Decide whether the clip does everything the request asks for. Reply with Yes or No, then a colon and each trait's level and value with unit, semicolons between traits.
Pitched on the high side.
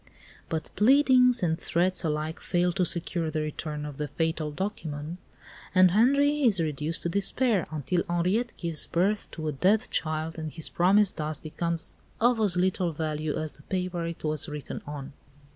No: medium, 170 Hz